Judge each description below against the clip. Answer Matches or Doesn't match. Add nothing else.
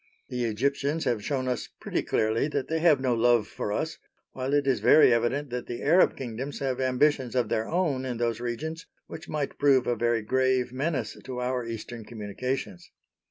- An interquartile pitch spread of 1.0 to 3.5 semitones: Matches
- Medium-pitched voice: Doesn't match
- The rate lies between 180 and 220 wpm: Matches